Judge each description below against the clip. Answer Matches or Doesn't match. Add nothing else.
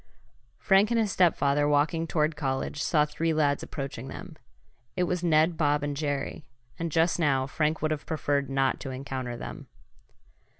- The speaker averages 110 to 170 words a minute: Matches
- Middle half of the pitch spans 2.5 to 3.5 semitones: Matches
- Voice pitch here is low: Doesn't match